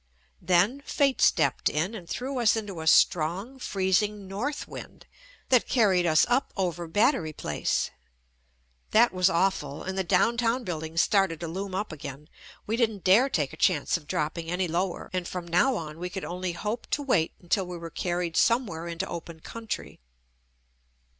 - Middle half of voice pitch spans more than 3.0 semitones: Yes, average, 4.6 semitones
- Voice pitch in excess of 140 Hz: Yes, medium, 185 Hz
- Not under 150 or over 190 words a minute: Yes, average, 180 wpm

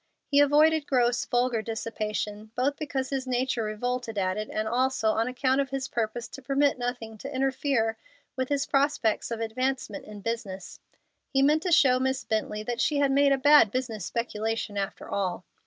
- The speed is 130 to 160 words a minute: No, average, 180 wpm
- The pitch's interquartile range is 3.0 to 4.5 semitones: Yes, average, 3.6 semitones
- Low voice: No, very high, 250 Hz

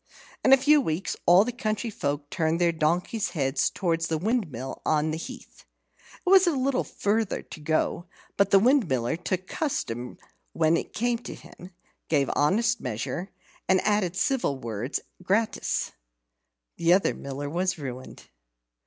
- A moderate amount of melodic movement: No, wide, 6.8 semitones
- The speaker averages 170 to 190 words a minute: No, average, 155 wpm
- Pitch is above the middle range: No, medium, 175 Hz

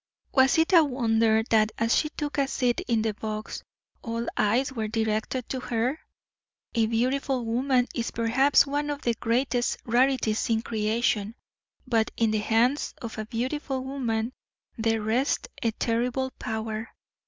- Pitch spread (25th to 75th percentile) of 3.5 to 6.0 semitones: No, average, 2.9 semitones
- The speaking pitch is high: Yes, high, 235 Hz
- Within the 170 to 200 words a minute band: No, average, 155 wpm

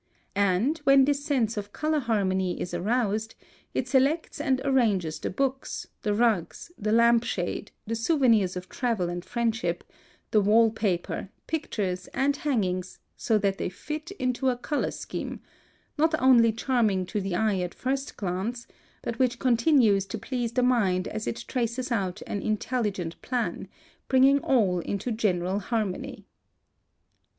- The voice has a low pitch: No, high, 225 Hz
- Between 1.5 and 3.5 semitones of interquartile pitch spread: No, average, 4.7 semitones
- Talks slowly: No, average, 150 wpm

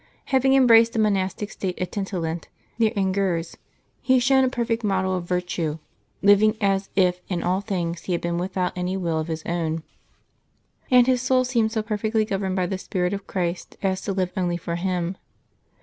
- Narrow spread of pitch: No, average, 3.5 semitones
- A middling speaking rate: Yes, average, 190 wpm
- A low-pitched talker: No, high, 190 Hz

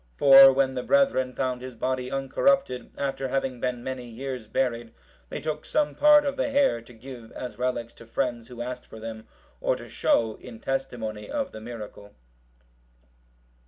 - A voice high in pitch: No, low, 125 Hz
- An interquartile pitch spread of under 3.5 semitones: Yes, narrow, 2.6 semitones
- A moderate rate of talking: Yes, average, 170 wpm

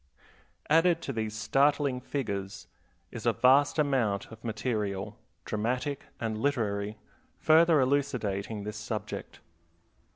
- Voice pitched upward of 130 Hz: No, low, 115 Hz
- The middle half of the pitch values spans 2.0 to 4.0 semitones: No, average, 5.1 semitones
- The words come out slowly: Yes, slow, 105 wpm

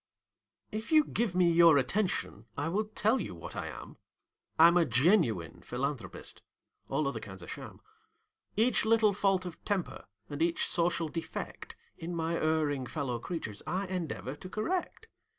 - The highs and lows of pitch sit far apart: Yes, wide, 5.7 semitones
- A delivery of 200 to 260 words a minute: No, average, 155 wpm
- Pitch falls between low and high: Yes, medium, 170 Hz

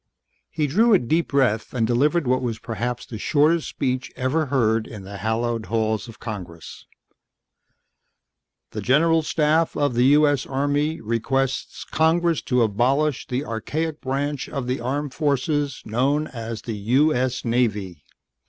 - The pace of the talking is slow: No, average, 145 wpm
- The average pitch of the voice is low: Yes, low, 130 Hz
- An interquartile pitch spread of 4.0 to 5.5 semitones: Yes, average, 4.4 semitones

